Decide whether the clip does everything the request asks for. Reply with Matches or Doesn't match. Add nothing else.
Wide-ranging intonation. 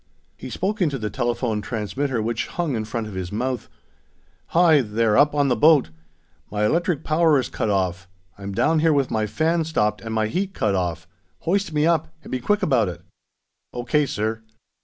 Matches